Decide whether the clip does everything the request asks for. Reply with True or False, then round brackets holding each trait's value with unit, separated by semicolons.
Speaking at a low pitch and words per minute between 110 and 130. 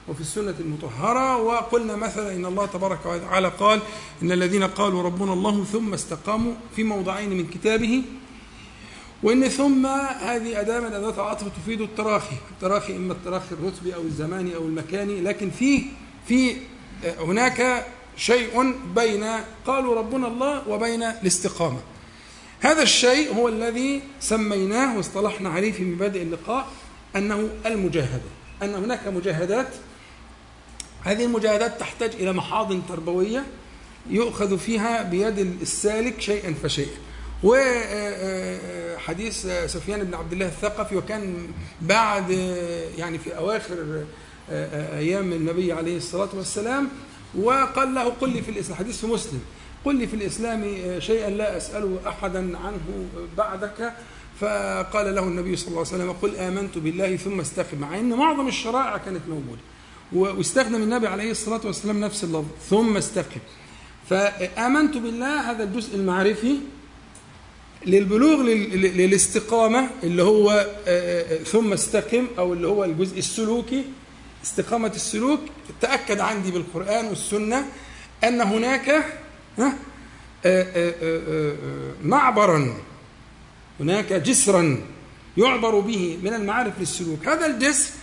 False (205 Hz; 115 wpm)